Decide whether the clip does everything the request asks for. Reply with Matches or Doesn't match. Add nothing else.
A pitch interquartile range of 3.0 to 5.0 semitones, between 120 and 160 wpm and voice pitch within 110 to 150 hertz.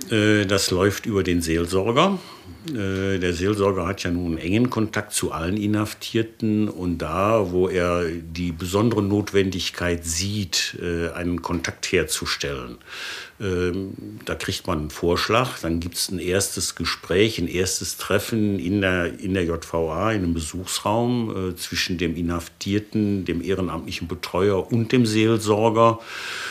Doesn't match